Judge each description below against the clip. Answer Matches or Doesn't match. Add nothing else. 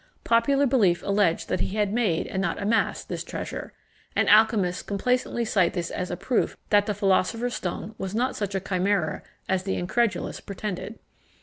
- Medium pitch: Doesn't match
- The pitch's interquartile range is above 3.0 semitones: Matches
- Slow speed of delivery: Doesn't match